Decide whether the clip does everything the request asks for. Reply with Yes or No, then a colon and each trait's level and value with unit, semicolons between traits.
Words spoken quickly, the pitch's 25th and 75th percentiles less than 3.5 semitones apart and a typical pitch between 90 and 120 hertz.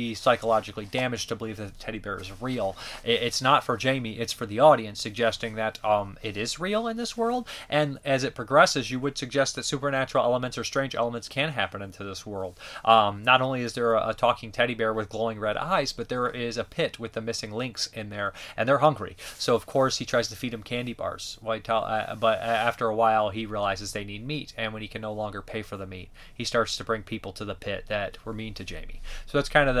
Yes: fast, 240 wpm; average, 2.9 semitones; low, 115 Hz